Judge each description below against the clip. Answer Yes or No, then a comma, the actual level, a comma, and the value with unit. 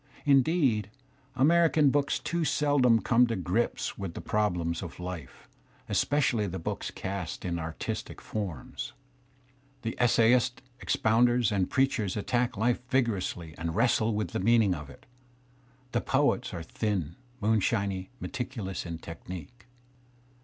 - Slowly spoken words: Yes, slow, 130 wpm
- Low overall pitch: Yes, low, 110 Hz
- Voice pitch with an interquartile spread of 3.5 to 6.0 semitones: Yes, average, 5.2 semitones